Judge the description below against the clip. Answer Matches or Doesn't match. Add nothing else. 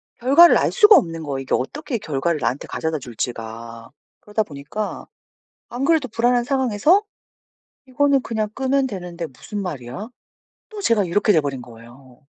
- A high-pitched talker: Matches